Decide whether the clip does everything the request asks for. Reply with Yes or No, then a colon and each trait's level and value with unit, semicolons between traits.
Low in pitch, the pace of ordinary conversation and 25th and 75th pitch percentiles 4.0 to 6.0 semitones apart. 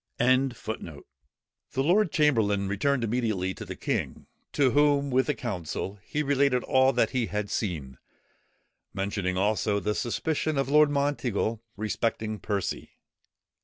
No: low, 115 Hz; slow, 130 wpm; wide, 5.4 semitones